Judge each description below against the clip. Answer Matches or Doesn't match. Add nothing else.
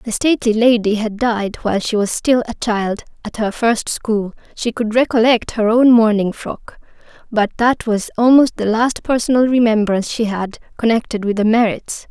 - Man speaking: Doesn't match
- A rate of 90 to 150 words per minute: Doesn't match